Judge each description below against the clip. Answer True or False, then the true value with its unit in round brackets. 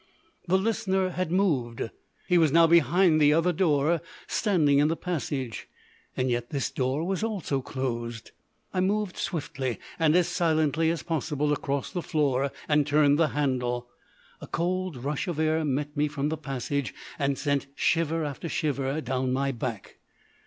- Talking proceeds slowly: False (160 wpm)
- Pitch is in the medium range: True (150 Hz)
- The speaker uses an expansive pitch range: False (3.7 semitones)